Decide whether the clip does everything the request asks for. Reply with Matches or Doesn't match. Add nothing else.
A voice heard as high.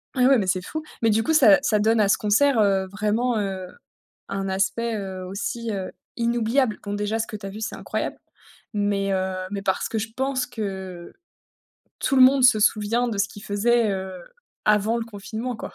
Matches